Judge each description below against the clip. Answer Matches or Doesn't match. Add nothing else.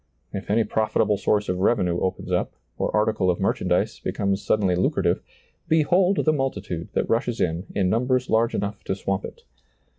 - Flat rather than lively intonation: Doesn't match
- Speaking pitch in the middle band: Doesn't match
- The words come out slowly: Doesn't match